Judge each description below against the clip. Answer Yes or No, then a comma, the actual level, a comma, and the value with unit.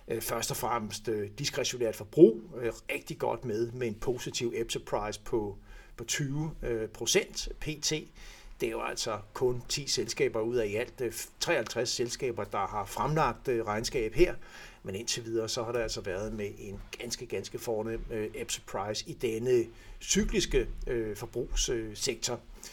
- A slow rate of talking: Yes, slow, 140 wpm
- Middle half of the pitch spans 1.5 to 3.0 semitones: No, average, 4.3 semitones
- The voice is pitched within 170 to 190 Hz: No, low, 115 Hz